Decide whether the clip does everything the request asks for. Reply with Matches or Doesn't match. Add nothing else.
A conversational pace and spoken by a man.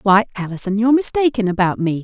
Doesn't match